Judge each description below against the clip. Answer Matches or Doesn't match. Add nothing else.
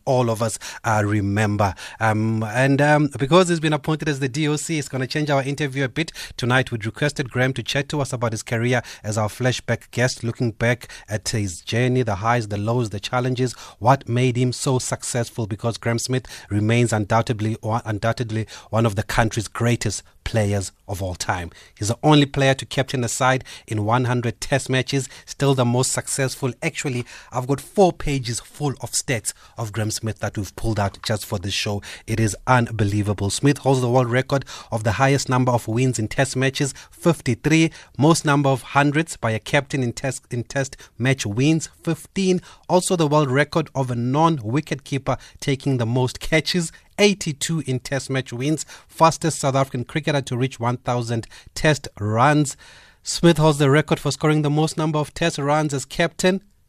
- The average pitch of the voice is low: Matches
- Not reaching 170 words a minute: Doesn't match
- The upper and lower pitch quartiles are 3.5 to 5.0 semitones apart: Matches